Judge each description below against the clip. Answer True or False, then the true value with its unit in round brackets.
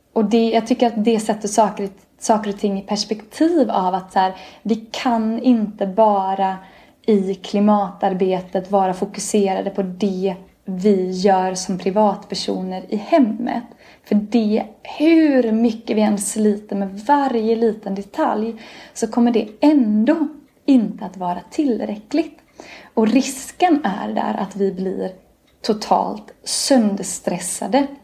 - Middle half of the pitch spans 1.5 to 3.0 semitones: False (3.4 semitones)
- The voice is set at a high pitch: True (215 Hz)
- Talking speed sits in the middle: False (130 wpm)